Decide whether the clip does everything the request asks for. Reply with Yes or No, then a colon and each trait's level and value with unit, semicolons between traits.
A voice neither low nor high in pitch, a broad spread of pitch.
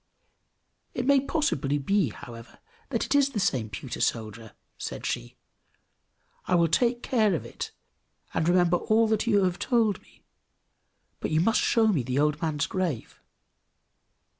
Yes: medium, 175 Hz; wide, 7.7 semitones